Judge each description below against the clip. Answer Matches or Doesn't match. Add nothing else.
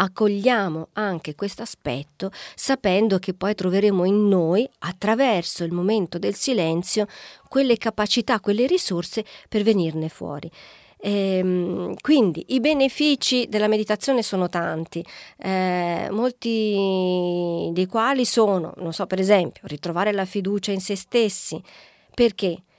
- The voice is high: Matches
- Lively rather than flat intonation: Doesn't match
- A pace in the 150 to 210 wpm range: Doesn't match